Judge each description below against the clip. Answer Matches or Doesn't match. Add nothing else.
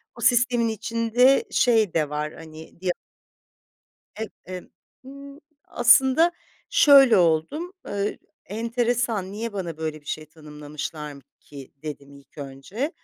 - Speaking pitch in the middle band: Doesn't match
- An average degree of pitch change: Doesn't match